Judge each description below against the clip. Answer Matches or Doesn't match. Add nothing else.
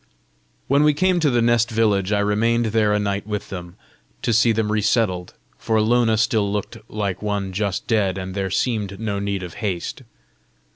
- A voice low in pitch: Matches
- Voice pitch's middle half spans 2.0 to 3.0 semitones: Matches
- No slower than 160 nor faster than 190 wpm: Matches